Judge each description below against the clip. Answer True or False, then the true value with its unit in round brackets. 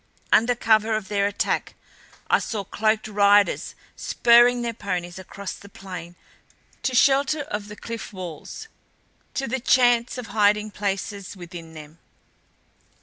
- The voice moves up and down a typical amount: True (3.4 semitones)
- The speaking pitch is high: True (210 Hz)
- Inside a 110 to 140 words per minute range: True (135 wpm)